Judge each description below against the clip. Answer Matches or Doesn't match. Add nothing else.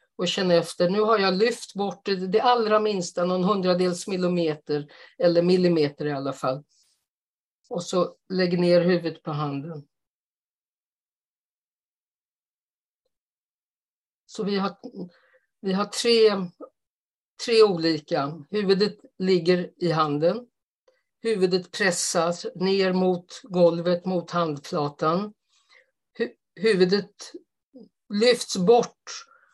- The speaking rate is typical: Doesn't match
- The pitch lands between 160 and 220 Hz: Matches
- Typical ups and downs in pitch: Matches